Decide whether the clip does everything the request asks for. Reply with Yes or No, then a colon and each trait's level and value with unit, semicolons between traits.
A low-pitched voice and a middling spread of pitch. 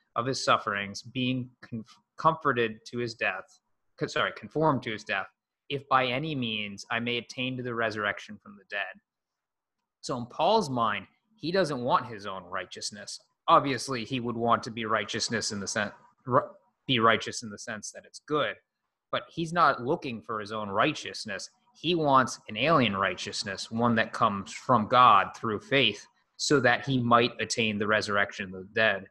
Yes: low, 120 Hz; average, 3.5 semitones